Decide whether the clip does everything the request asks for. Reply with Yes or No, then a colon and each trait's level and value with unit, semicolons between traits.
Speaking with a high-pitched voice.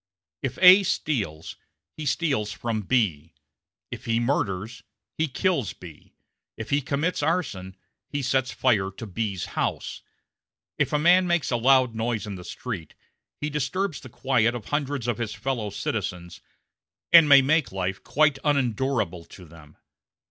No: low, 120 Hz